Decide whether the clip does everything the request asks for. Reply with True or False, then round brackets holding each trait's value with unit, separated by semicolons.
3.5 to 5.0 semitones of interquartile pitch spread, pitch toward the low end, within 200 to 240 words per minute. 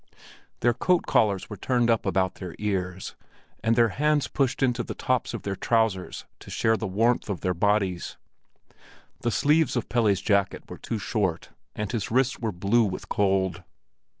False (3.8 semitones; 105 Hz; 175 wpm)